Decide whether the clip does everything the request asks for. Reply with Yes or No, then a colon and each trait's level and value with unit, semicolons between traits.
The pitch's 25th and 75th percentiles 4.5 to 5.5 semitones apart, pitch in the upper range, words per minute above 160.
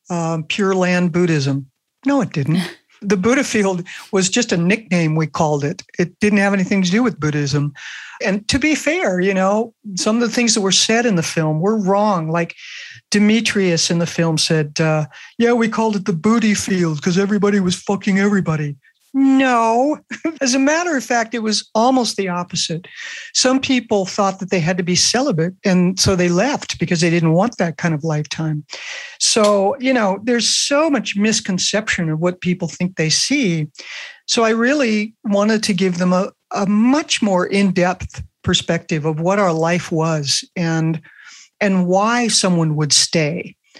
Yes: average, 5.0 semitones; high, 195 Hz; average, 180 wpm